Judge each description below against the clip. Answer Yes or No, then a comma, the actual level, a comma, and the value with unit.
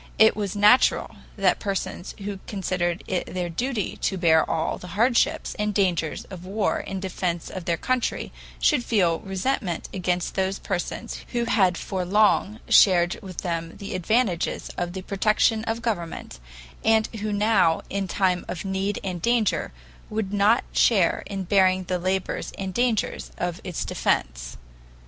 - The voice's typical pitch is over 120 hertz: Yes, high, 190 Hz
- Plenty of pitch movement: No, average, 3.0 semitones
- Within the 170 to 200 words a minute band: No, average, 155 wpm